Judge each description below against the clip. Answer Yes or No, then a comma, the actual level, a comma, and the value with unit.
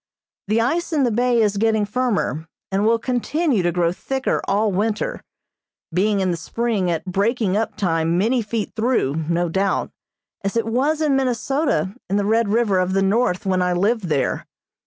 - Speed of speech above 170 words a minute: Yes, average, 180 wpm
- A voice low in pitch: No, high, 210 Hz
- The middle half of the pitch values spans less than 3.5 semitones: No, average, 4.3 semitones